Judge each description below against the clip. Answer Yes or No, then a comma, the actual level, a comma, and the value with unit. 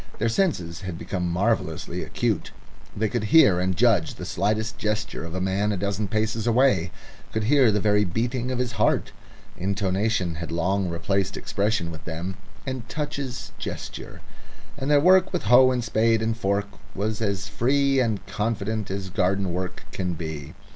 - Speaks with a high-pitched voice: No, low, 105 Hz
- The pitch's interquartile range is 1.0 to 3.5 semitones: No, average, 3.9 semitones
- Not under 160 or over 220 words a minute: Yes, average, 170 wpm